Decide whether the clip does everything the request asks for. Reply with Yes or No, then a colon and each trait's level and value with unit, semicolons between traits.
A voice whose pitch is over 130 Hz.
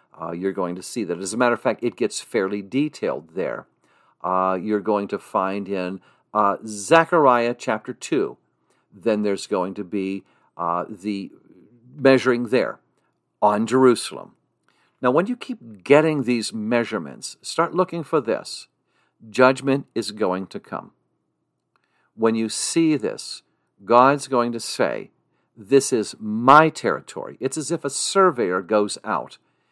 No: low, 115 Hz